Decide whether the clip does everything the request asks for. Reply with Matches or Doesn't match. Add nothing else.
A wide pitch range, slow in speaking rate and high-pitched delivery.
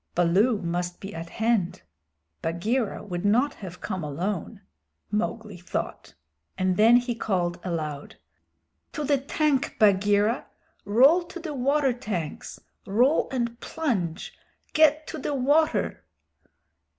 Matches